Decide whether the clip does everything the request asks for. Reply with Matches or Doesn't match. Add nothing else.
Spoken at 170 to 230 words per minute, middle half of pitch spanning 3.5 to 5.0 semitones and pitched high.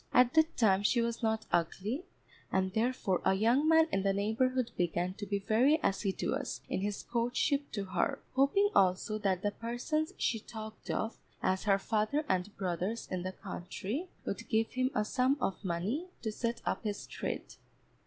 Matches